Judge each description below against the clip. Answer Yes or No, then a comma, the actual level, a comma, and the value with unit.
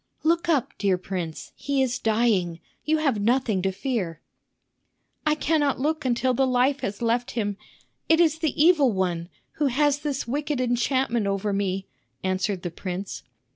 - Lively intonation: Yes, wide, 6.5 semitones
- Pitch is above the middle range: Yes, high, 240 Hz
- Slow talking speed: No, average, 160 wpm